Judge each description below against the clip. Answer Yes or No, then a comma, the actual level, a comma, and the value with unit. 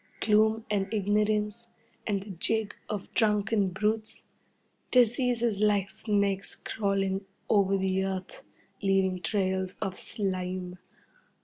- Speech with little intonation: Yes, narrow, 2.1 semitones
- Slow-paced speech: Yes, slow, 105 wpm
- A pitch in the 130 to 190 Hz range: No, high, 200 Hz